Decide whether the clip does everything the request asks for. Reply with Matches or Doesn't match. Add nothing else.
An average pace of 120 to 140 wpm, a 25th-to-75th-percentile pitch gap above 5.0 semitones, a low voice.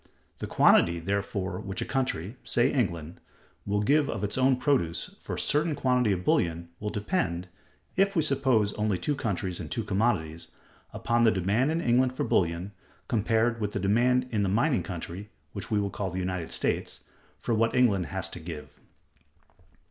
Doesn't match